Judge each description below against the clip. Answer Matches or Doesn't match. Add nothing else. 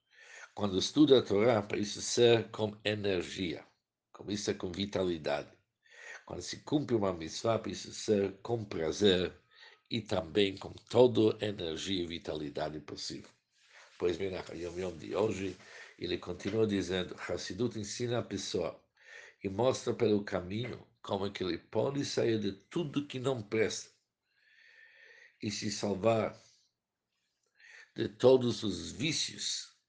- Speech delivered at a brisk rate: Doesn't match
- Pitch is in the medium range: Doesn't match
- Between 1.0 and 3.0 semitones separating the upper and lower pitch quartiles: Doesn't match